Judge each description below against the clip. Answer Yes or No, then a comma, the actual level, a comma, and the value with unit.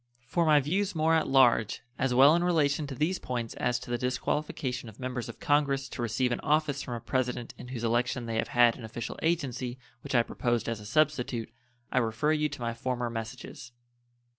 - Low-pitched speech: Yes, low, 125 Hz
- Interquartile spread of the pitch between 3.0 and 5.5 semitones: Yes, average, 3.6 semitones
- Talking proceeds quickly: Yes, fast, 210 wpm